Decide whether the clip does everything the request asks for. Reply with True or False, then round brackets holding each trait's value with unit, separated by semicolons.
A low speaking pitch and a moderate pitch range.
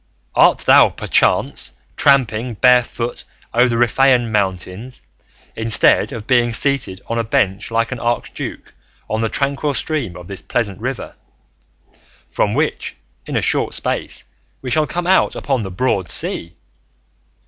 True (120 Hz; 3.4 semitones)